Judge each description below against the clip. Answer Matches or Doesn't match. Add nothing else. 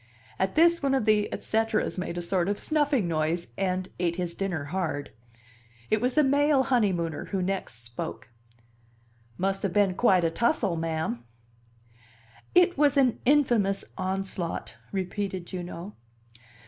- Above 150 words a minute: Doesn't match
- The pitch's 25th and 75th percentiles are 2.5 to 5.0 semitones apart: Doesn't match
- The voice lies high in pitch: Matches